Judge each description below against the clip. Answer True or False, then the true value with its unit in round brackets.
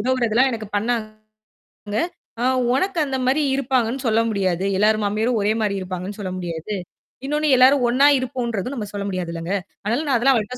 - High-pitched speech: True (225 Hz)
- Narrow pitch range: False (4.2 semitones)